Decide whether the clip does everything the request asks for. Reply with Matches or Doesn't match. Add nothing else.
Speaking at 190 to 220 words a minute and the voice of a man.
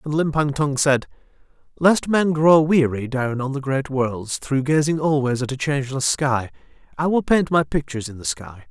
Matches